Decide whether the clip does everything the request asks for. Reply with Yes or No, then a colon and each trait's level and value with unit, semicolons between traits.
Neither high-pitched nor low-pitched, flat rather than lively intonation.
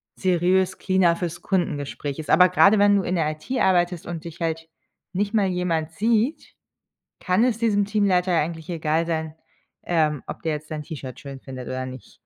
No: medium, 170 Hz; average, 3.5 semitones